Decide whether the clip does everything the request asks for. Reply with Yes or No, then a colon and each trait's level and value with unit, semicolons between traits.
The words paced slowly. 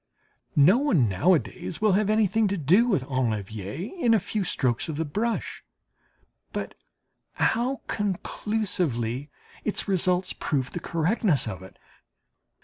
Yes: slow, 130 wpm